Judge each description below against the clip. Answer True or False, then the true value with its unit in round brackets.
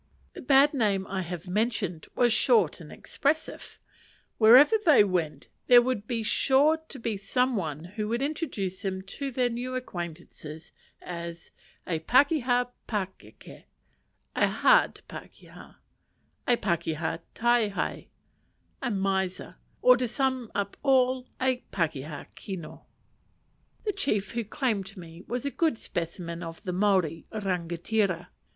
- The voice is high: True (210 Hz)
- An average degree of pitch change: False (6.1 semitones)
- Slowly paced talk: True (130 wpm)